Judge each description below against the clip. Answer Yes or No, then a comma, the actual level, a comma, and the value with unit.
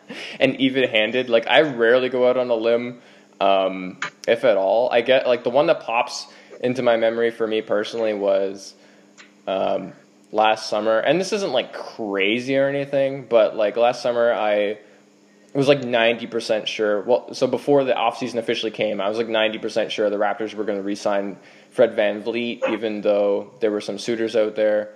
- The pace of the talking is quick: No, average, 190 wpm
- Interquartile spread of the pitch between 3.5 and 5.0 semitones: No, average, 2.8 semitones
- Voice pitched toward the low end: Yes, low, 110 Hz